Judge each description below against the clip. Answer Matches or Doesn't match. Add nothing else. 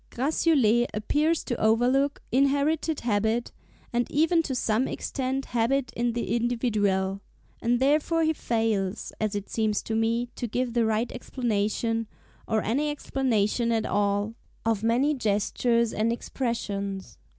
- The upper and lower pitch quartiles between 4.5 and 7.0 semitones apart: Doesn't match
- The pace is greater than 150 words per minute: Doesn't match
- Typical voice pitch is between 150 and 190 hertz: Doesn't match